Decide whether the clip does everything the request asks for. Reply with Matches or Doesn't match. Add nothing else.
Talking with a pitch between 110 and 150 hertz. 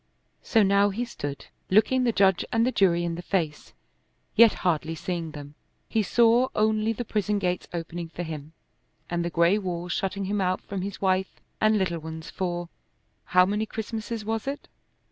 Doesn't match